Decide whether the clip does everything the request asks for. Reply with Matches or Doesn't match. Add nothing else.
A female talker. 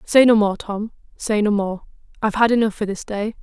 Matches